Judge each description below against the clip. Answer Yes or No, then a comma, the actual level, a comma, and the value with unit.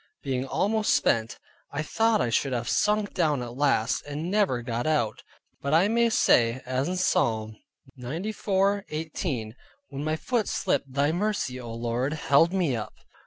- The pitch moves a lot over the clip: Yes, wide, 7.5 semitones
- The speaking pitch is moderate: Yes, medium, 145 Hz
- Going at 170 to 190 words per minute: No, average, 160 wpm